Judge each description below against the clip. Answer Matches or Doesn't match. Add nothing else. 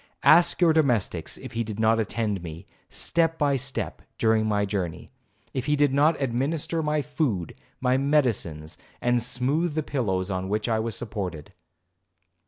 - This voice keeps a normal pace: Matches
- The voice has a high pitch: Doesn't match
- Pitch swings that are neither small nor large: Doesn't match